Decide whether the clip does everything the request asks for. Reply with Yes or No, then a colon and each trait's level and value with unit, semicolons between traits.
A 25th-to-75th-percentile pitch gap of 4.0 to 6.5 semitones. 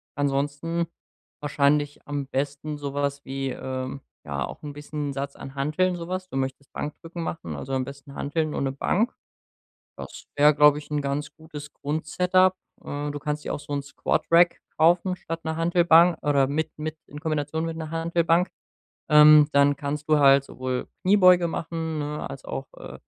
No: average, 2.7 semitones